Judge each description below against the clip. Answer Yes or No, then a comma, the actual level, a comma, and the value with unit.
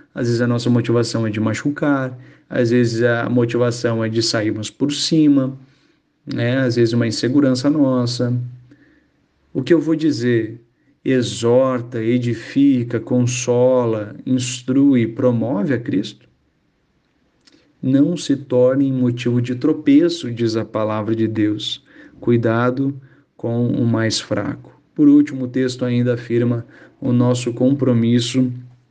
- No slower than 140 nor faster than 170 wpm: No, average, 125 wpm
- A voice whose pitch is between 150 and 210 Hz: No, low, 125 Hz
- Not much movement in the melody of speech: Yes, narrow, 2.2 semitones